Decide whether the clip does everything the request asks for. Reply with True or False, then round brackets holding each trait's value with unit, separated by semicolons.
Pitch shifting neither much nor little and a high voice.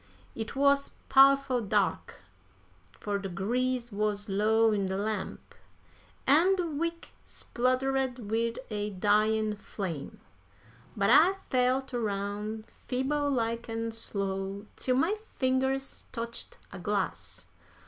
True (4.5 semitones; 225 Hz)